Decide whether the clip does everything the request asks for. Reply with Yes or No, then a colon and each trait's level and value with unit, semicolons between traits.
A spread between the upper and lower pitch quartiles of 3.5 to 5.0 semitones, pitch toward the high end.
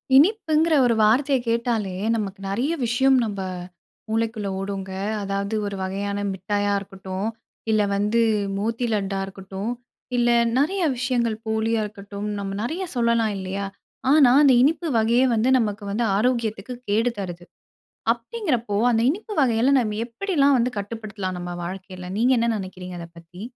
Yes: average, 3.8 semitones; high, 220 Hz